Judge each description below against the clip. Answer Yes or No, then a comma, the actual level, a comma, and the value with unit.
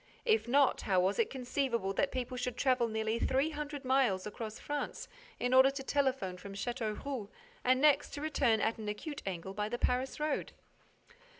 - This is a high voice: Yes, very high, 250 Hz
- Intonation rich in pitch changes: No, average, 4.4 semitones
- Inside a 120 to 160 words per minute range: No, average, 180 wpm